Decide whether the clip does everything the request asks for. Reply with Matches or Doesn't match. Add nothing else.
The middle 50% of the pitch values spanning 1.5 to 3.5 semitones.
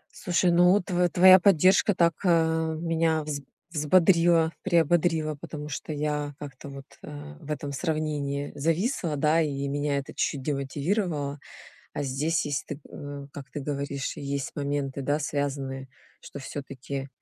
Matches